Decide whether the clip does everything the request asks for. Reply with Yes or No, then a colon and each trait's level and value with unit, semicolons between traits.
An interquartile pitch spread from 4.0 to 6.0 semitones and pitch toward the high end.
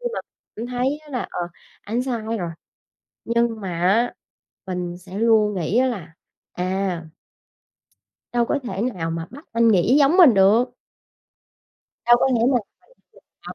Yes: average, 4.9 semitones; high, 225 Hz